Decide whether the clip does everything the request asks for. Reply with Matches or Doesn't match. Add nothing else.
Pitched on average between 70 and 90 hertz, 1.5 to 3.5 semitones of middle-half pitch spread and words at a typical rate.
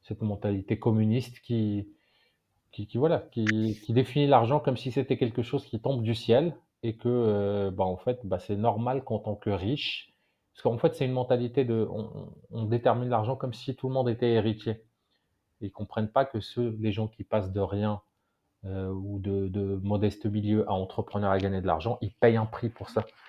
Doesn't match